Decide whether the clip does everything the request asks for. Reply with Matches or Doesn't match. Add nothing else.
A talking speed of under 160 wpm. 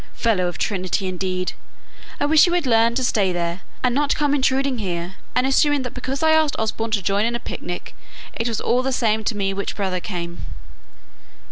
Doesn't match